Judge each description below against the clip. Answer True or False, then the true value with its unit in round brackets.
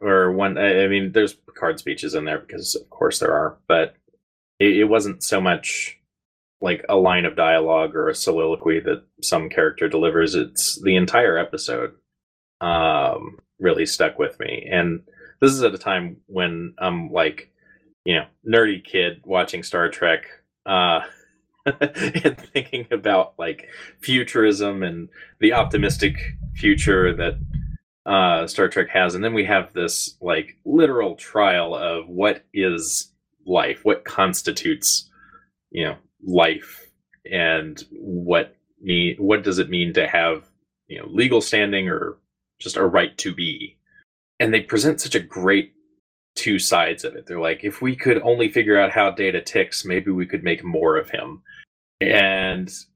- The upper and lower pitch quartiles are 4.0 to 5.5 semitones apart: True (4.3 semitones)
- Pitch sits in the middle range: False (95 Hz)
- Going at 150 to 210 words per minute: True (155 wpm)